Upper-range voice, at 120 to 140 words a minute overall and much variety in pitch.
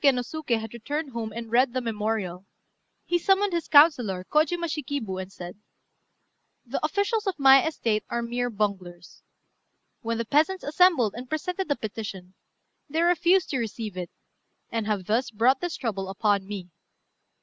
No: high, 235 Hz; average, 170 wpm; wide, 6.8 semitones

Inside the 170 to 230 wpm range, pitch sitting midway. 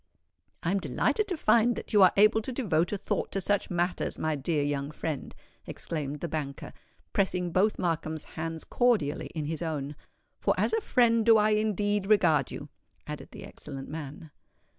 Yes: average, 180 wpm; medium, 175 Hz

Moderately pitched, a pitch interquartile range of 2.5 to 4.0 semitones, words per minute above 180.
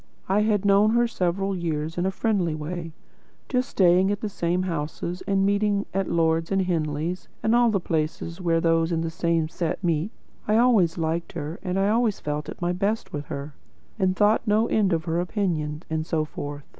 Yes: medium, 175 Hz; average, 3.6 semitones; average, 200 wpm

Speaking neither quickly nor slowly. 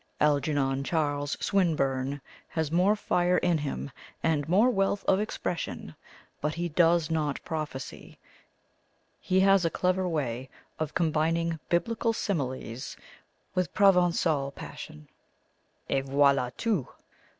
No: slow, 115 wpm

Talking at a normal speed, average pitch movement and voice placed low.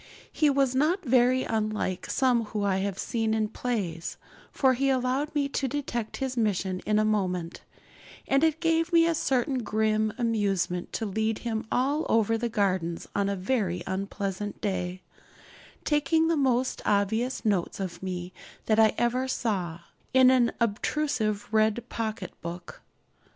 No: average, 155 wpm; average, 4.7 semitones; high, 220 Hz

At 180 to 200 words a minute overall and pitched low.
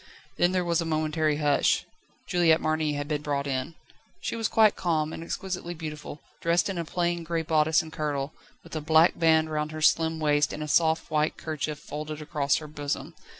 No: average, 195 wpm; medium, 155 Hz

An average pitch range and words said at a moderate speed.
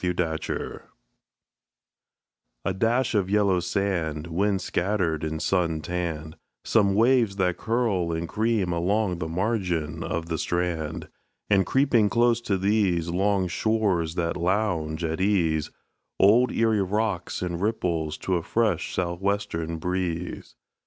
No: average, 3.8 semitones; slow, 130 wpm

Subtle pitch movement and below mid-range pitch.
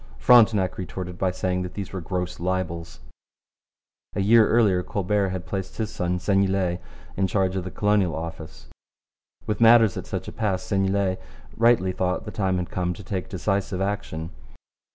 Yes: narrow, 2.1 semitones; very low, 95 Hz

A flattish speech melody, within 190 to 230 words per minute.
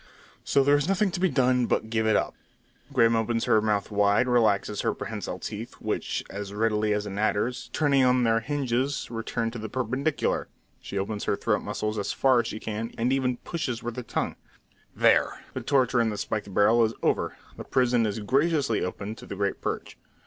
No: average, 3.2 semitones; average, 200 wpm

